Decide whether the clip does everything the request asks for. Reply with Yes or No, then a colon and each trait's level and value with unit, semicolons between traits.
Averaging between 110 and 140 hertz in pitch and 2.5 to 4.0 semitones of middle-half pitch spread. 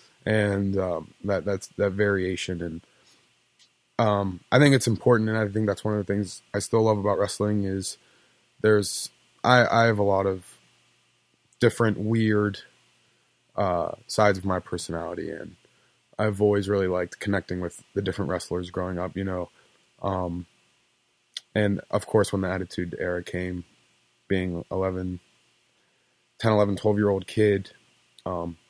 No: very low, 95 Hz; average, 2.8 semitones